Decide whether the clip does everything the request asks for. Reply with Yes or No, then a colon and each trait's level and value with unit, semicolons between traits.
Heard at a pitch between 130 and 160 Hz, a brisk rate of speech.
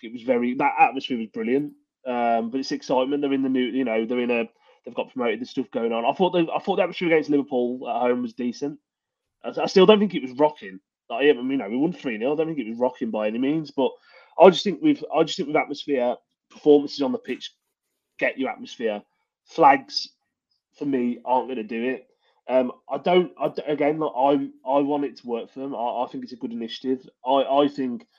Yes: medium, 140 Hz; fast, 240 wpm